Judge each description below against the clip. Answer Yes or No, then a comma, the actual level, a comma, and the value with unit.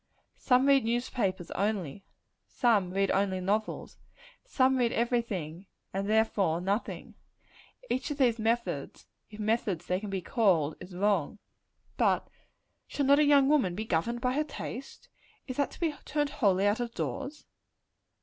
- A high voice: Yes, high, 220 Hz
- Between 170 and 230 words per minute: No, average, 155 wpm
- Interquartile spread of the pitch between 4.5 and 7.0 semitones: Yes, average, 5.1 semitones